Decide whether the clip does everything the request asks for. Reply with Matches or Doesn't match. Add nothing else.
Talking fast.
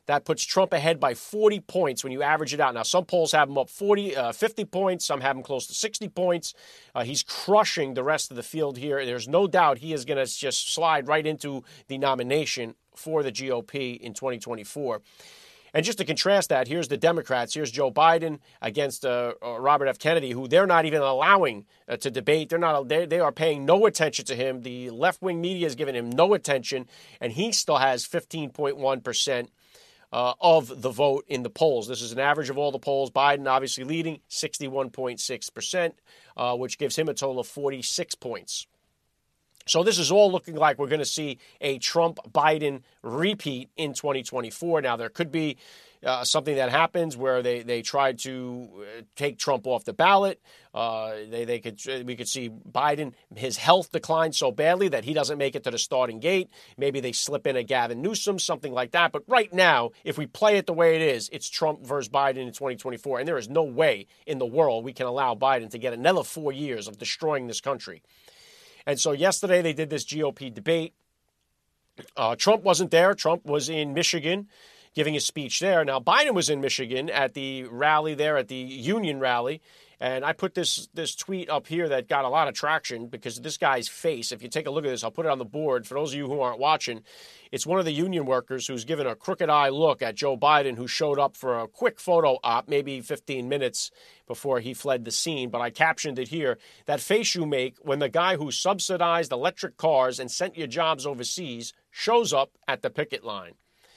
Matches